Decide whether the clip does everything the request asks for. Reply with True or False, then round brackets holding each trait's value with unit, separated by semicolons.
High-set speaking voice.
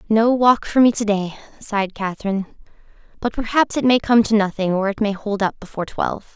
True (210 Hz)